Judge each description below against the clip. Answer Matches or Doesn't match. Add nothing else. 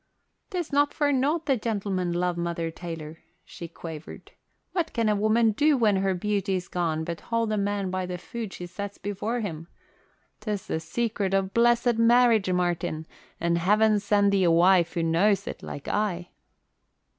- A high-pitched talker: Matches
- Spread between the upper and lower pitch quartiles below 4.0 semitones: Doesn't match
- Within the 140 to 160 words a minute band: Doesn't match